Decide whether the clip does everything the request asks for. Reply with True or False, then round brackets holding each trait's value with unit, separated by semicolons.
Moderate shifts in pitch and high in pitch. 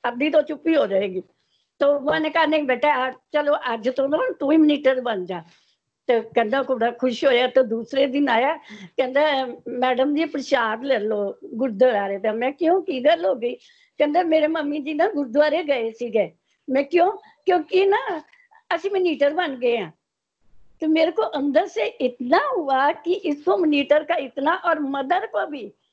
True (4.1 semitones; 285 Hz)